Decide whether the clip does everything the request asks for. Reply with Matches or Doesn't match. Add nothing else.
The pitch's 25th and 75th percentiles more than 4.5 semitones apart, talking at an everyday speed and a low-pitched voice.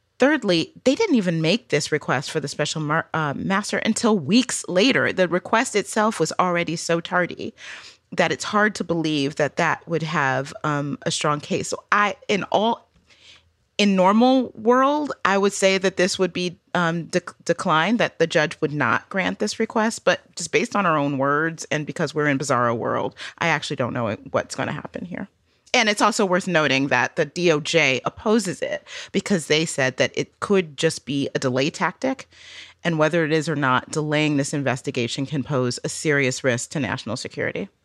Doesn't match